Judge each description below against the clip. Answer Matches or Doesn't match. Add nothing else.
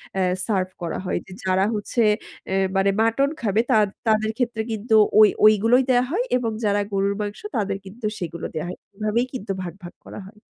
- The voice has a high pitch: Matches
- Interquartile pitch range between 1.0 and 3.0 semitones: Matches